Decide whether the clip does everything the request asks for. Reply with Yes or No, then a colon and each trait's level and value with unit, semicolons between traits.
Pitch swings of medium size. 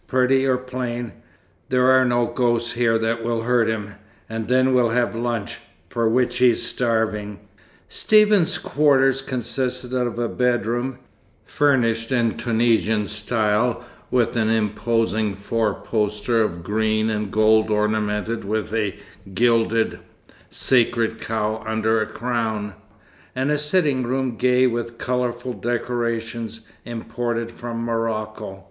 No: narrow, 2.1 semitones